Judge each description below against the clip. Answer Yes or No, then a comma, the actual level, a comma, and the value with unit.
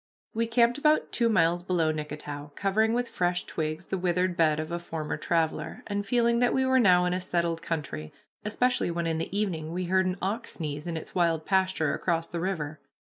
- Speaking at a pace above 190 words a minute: Yes, fast, 205 wpm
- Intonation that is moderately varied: Yes, average, 4.0 semitones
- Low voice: No, medium, 175 Hz